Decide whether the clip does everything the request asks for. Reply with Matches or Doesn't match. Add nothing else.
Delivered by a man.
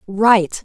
Doesn't match